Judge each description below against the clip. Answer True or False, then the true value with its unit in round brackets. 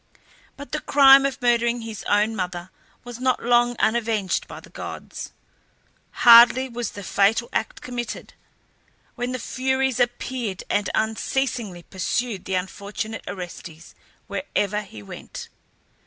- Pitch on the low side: False (230 Hz)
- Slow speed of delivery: True (125 wpm)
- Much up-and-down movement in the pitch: False (3.7 semitones)